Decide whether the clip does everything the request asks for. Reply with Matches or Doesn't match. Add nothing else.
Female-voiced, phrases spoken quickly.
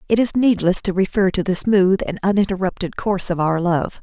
Matches